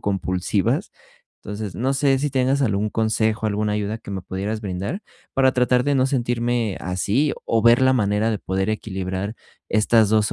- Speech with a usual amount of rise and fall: Yes, average, 3.7 semitones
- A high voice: No, low, 110 Hz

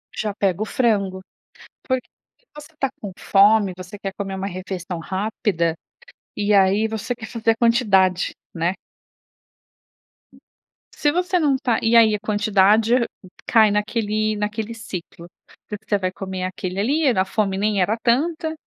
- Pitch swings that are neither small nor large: Yes, average, 3.2 semitones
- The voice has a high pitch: Yes, high, 210 Hz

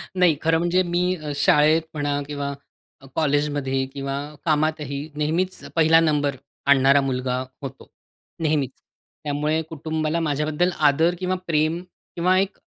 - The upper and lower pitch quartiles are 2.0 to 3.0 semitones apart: Yes, narrow, 2.5 semitones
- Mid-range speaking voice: Yes, medium, 155 Hz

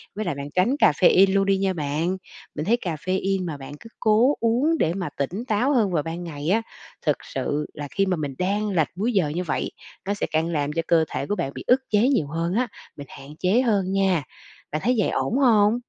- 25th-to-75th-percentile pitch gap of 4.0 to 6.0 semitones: Yes, average, 5.2 semitones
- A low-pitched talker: No, medium, 185 Hz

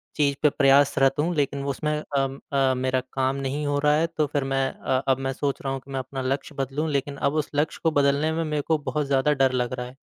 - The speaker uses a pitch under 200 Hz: Yes, medium, 140 Hz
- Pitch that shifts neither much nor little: No, narrow, 1.7 semitones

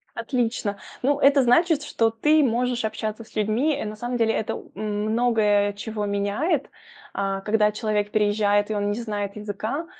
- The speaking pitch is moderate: No, high, 220 Hz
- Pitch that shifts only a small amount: No, average, 3.0 semitones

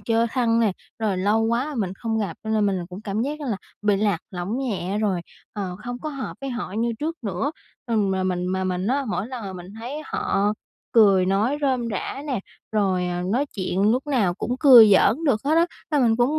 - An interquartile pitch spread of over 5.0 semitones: No, average, 4.6 semitones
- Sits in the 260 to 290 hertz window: No, high, 220 Hz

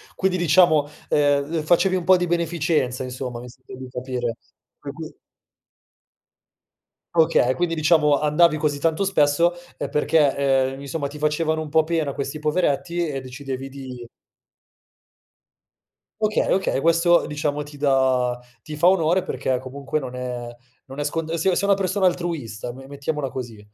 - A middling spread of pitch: Yes, average, 4.0 semitones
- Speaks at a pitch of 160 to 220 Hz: No, medium, 150 Hz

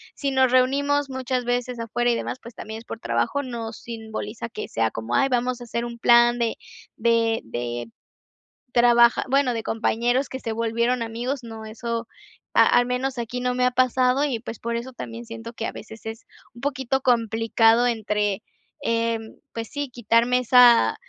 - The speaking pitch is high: Yes, high, 235 Hz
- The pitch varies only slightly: Yes, narrow, 1.9 semitones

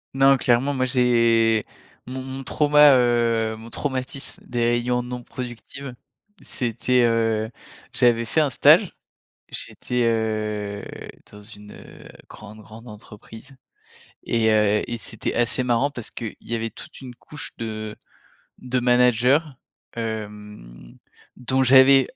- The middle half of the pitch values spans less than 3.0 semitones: Yes, narrow, 2.5 semitones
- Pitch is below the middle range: Yes, low, 120 Hz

